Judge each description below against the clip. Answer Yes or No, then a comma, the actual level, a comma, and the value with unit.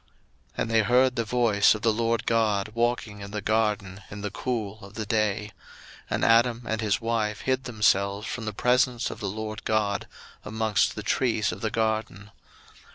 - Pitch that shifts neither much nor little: No, narrow, 2.0 semitones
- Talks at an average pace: Yes, average, 185 wpm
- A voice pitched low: Yes, low, 110 Hz